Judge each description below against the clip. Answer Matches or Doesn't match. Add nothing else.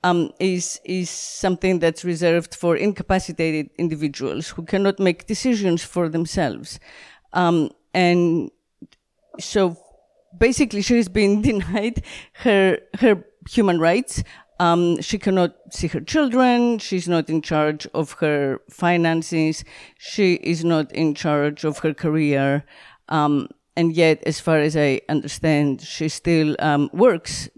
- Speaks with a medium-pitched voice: Matches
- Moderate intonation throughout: Matches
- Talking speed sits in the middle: Doesn't match